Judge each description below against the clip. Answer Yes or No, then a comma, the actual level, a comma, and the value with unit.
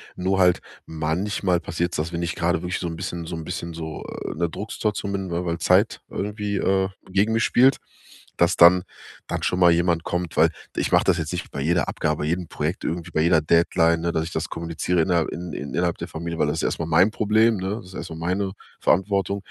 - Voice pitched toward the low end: Yes, very low, 85 Hz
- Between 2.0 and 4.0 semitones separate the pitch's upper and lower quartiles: Yes, narrow, 2.4 semitones